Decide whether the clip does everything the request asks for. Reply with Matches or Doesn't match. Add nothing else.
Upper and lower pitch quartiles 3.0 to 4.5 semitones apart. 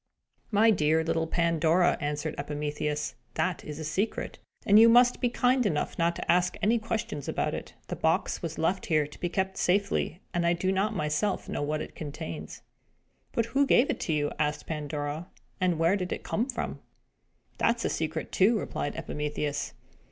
Doesn't match